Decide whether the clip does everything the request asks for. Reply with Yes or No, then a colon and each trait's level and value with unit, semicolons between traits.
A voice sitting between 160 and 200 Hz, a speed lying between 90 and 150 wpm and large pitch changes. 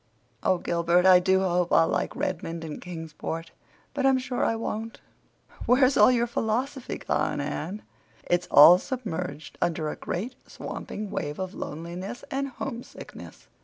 Yes: medium, 185 Hz; average, 145 wpm; wide, 6.1 semitones